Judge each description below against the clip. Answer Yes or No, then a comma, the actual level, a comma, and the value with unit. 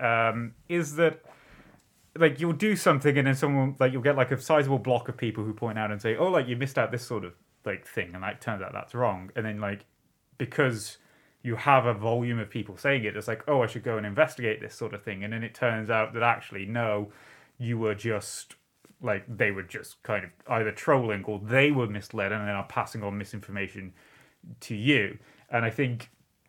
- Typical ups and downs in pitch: Yes, average, 4.3 semitones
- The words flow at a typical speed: No, fast, 220 wpm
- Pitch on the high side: No, low, 115 Hz